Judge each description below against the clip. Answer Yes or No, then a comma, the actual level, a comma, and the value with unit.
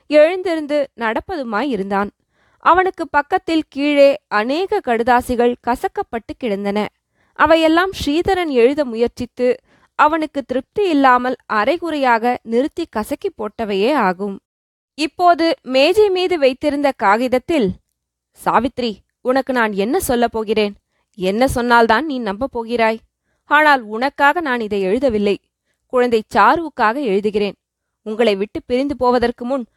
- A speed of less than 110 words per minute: Yes, average, 100 wpm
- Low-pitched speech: No, very high, 255 Hz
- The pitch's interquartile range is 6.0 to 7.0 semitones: No, average, 5.1 semitones